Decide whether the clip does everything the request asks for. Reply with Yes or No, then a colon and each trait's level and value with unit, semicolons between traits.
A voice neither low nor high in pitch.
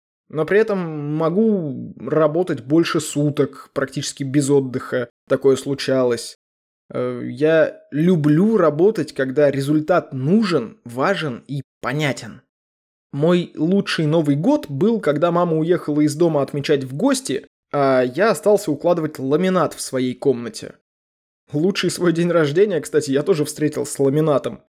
Yes: medium, 150 Hz